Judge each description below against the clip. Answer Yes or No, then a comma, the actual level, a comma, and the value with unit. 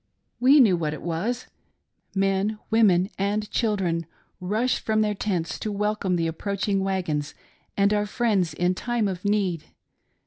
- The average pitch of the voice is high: Yes, high, 200 Hz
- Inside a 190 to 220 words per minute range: No, average, 145 wpm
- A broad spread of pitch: No, average, 3.2 semitones